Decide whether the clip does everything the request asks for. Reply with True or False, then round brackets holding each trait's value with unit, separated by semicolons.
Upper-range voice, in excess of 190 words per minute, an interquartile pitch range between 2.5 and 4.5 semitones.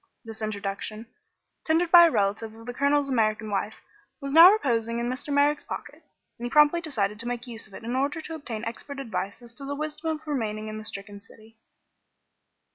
False (240 Hz; 200 wpm; 5.1 semitones)